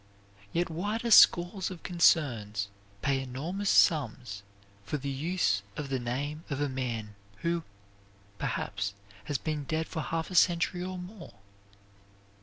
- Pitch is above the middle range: No, medium, 150 Hz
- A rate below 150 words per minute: Yes, average, 140 wpm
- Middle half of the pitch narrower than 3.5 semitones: No, average, 5.2 semitones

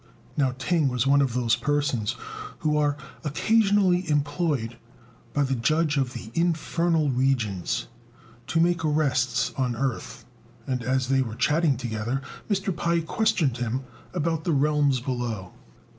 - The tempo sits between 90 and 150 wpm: Yes, average, 140 wpm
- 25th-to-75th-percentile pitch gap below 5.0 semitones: Yes, average, 4.6 semitones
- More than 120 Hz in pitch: Yes, medium, 140 Hz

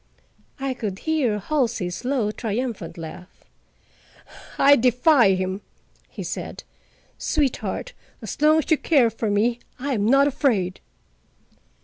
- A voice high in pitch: Yes, high, 240 Hz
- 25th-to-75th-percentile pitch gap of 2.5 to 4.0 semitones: No, wide, 5.5 semitones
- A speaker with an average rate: No, slow, 120 wpm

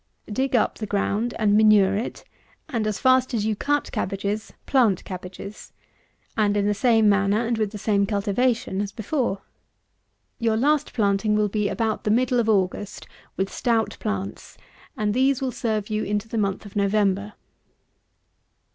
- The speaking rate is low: No, average, 165 wpm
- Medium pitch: No, high, 215 Hz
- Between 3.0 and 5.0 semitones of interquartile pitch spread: No, narrow, 2.5 semitones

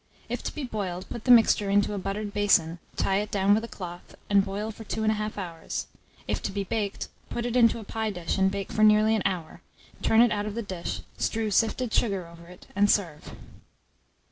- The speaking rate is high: Yes, fast, 220 wpm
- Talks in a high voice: Yes, high, 205 Hz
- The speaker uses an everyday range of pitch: No, narrow, 2.3 semitones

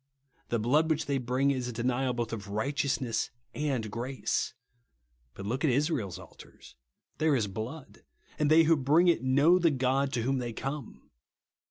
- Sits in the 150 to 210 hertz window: No, low, 130 Hz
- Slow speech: No, average, 170 wpm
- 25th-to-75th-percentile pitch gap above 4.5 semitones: No, average, 3.8 semitones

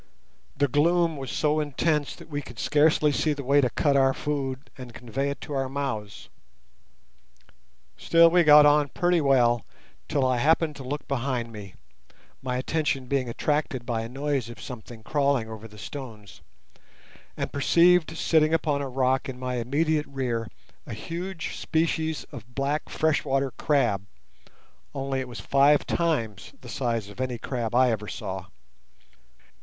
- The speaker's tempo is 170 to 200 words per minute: No, average, 155 wpm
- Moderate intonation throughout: Yes, average, 3.6 semitones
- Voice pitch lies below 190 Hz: Yes, low, 135 Hz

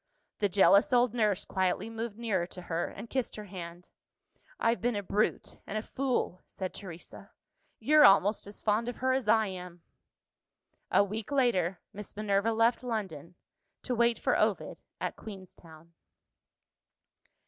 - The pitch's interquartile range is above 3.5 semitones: Yes, average, 3.9 semitones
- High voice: Yes, high, 210 Hz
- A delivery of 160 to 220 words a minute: No, average, 150 wpm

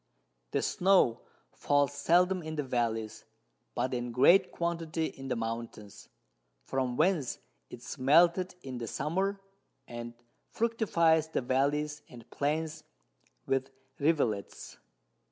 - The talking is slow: Yes, slow, 120 wpm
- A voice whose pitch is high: No, medium, 145 Hz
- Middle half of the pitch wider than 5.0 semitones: Yes, wide, 5.5 semitones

